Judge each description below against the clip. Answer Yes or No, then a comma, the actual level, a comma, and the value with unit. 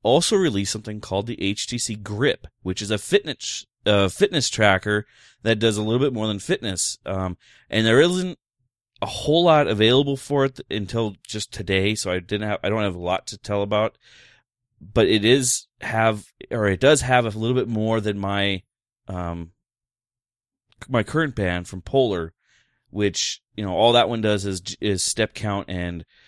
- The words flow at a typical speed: Yes, average, 185 wpm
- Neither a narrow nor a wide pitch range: Yes, average, 3.3 semitones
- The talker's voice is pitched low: Yes, low, 105 Hz